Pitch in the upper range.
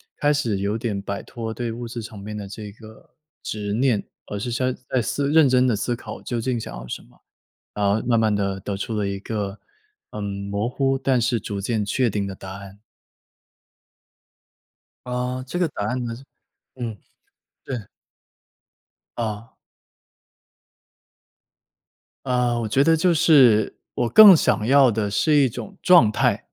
No: low, 115 Hz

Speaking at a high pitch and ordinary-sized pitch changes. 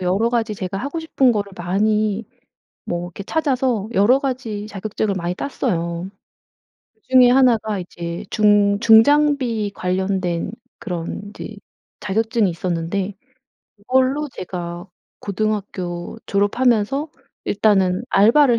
Yes: high, 210 Hz; average, 4.5 semitones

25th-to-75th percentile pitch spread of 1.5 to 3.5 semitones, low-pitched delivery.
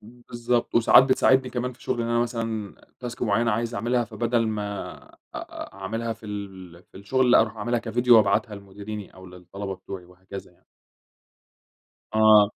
Yes: average, 3.1 semitones; low, 110 Hz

